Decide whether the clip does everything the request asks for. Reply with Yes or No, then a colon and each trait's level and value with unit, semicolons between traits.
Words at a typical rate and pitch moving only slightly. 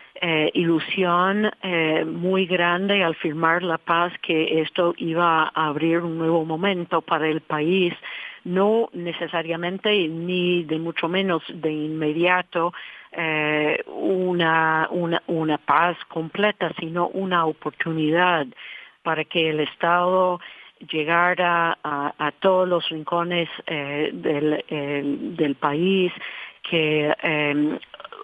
No: slow, 115 wpm; narrow, 2.1 semitones